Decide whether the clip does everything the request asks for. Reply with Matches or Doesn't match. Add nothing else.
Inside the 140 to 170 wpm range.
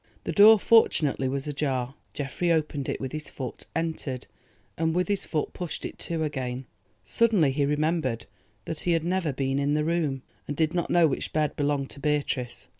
Doesn't match